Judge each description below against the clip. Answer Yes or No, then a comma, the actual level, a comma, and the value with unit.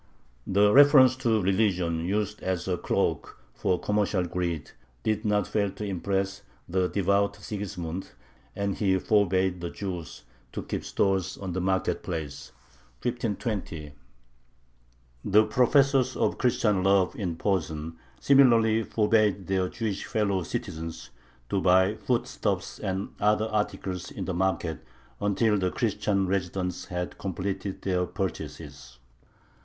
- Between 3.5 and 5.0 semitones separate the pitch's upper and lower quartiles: No, narrow, 2.6 semitones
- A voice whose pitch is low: Yes, very low, 95 Hz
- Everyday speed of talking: No, slow, 125 wpm